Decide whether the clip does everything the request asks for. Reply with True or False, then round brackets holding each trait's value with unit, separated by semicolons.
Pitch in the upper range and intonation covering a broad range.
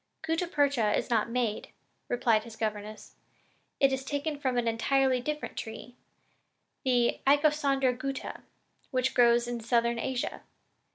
False (250 Hz; 2.8 semitones)